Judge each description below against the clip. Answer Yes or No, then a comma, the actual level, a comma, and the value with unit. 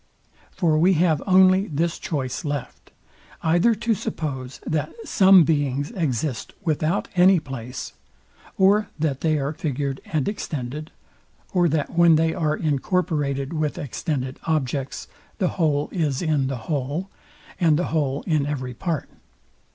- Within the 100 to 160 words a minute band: Yes, slow, 135 wpm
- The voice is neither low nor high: Yes, medium, 155 Hz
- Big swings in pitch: No, average, 3.6 semitones